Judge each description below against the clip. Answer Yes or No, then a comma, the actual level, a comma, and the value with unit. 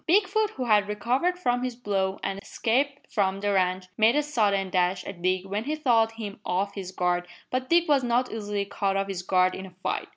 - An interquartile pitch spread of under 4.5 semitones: No, average, 4.8 semitones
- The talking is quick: Yes, fast, 220 wpm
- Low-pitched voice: No, high, 205 Hz